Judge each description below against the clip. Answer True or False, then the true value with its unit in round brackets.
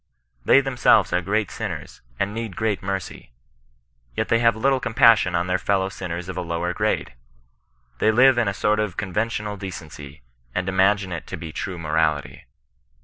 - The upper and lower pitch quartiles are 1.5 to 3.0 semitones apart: False (3.9 semitones)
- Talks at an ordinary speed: True (175 wpm)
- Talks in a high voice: False (95 Hz)